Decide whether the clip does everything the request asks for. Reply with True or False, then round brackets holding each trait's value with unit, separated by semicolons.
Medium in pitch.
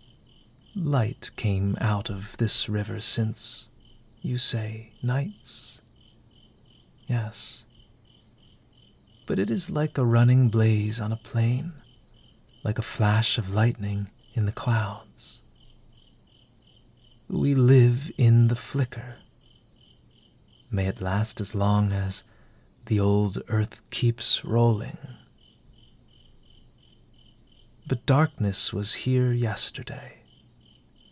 False (115 Hz)